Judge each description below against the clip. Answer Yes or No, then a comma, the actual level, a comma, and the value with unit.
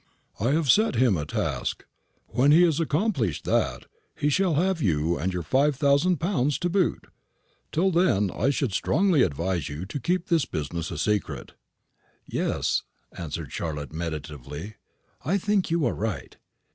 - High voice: No, low, 130 Hz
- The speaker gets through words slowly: No, average, 160 wpm